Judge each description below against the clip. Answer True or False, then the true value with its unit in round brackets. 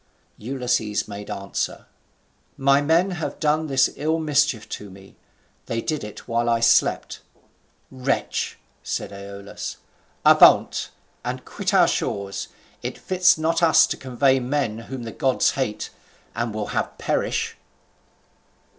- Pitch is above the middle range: False (130 Hz)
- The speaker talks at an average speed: False (130 wpm)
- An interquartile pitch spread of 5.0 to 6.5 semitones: True (5.6 semitones)